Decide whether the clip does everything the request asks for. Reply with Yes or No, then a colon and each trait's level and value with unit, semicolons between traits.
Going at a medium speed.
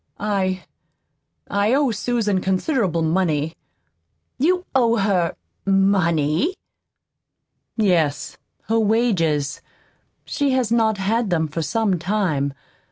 No: slow, 100 wpm